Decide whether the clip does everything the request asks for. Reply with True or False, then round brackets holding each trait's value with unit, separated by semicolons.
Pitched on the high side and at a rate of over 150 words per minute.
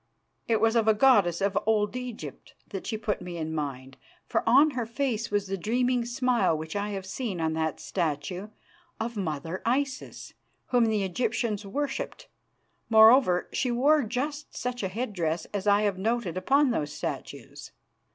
True (215 Hz; 170 wpm)